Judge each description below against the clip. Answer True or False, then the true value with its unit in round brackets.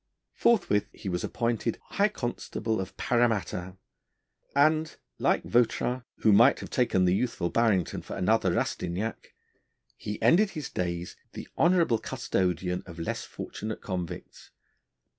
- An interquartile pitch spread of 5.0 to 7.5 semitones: True (5.5 semitones)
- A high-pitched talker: False (110 Hz)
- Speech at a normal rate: False (125 wpm)